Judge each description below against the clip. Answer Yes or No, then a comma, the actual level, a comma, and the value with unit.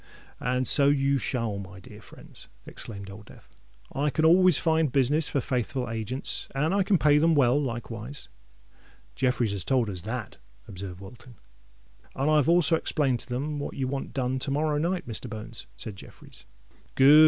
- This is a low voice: Yes, low, 130 Hz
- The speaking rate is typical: Yes, average, 170 wpm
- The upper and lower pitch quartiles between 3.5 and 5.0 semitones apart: Yes, average, 4.6 semitones